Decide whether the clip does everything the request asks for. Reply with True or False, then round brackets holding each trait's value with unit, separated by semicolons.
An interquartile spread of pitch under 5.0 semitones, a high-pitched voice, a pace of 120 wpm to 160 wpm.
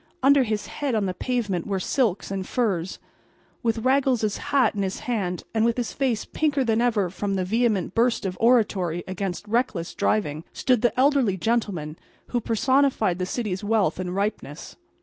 False (4.6 semitones; 215 Hz; 170 wpm)